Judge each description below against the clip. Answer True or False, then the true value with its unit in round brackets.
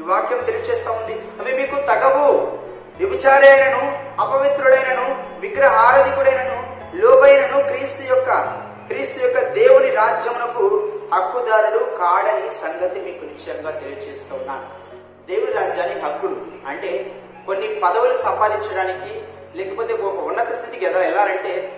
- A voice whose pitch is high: True (275 Hz)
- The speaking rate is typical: True (100 wpm)